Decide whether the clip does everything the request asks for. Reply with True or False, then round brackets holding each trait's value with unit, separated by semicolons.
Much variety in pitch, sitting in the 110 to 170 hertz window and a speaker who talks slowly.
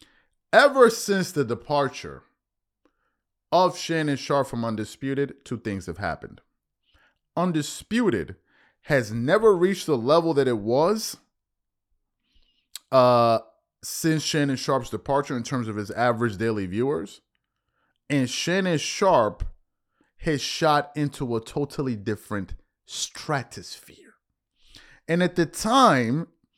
True (5.8 semitones; 140 Hz; 110 wpm)